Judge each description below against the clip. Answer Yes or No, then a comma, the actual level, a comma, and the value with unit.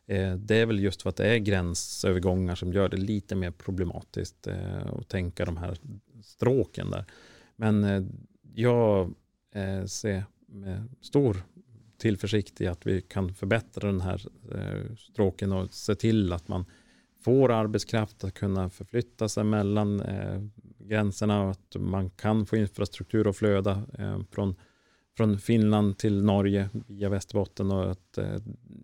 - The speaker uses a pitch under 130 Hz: Yes, low, 100 Hz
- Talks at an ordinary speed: Yes, average, 135 wpm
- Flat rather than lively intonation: Yes, narrow, 2.3 semitones